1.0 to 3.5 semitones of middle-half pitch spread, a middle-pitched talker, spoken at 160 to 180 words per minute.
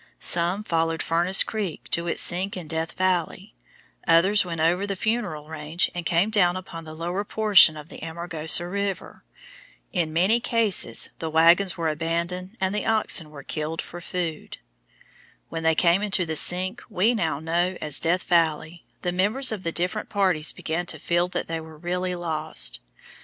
Yes: narrow, 2.6 semitones; medium, 175 Hz; average, 175 wpm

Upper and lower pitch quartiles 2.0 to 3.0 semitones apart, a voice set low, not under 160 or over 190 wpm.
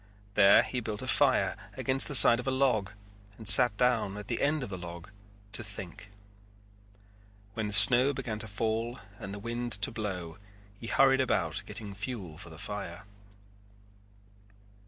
No: average, 3.7 semitones; low, 110 Hz; average, 165 wpm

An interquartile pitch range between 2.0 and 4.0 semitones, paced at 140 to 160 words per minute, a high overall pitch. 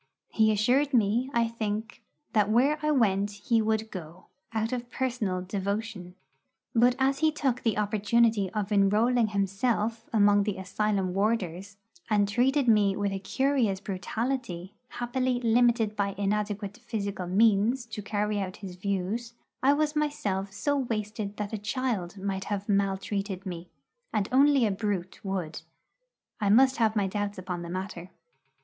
Yes: average, 3.2 semitones; average, 150 wpm; high, 210 Hz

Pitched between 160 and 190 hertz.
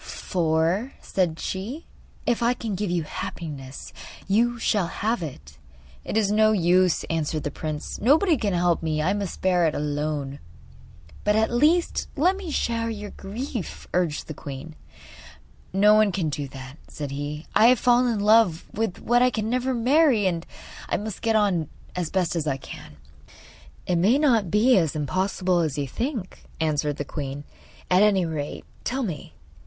Yes: medium, 185 Hz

